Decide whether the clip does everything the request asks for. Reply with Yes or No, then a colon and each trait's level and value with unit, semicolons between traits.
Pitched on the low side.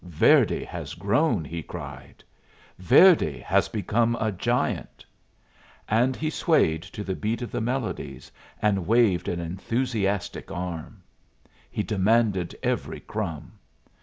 Yes: low, 105 Hz